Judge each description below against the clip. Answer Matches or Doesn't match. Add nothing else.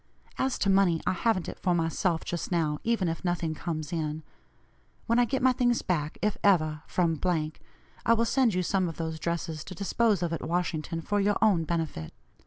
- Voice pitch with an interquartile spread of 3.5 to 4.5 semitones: Matches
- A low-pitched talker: Doesn't match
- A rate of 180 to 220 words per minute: Matches